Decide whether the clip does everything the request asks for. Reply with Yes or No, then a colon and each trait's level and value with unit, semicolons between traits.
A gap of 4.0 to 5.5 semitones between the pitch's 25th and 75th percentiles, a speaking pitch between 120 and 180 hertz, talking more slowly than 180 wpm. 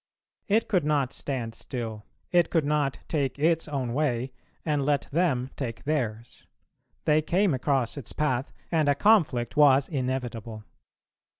No: average, 3.6 semitones; medium, 140 Hz; average, 140 wpm